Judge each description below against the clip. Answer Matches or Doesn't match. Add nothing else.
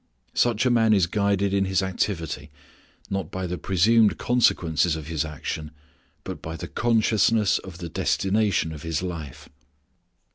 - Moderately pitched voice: Doesn't match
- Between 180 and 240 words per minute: Doesn't match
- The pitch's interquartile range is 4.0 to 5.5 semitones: Matches